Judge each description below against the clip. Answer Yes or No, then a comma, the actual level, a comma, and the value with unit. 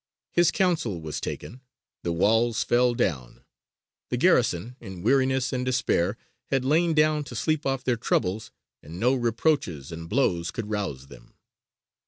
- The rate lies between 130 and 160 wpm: Yes, average, 150 wpm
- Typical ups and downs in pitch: No, wide, 6.9 semitones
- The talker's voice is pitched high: No, low, 120 Hz